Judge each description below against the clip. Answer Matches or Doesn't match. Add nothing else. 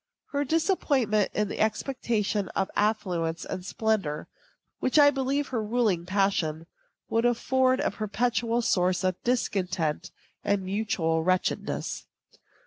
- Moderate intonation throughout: Matches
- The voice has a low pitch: Doesn't match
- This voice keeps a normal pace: Doesn't match